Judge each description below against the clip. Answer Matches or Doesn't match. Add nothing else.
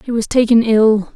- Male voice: Doesn't match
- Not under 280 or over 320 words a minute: Doesn't match